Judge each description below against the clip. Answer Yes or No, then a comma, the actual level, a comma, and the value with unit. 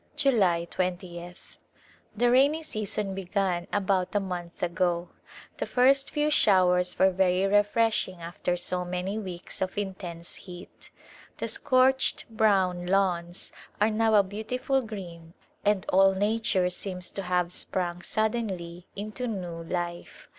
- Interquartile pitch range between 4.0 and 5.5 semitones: No, average, 3.2 semitones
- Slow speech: Yes, slow, 130 wpm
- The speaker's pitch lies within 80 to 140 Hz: No, high, 190 Hz